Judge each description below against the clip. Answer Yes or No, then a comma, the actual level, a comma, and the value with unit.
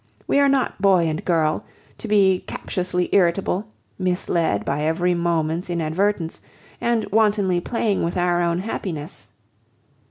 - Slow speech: Yes, slow, 130 wpm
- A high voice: No, medium, 180 Hz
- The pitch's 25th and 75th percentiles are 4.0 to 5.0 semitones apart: No, average, 3.1 semitones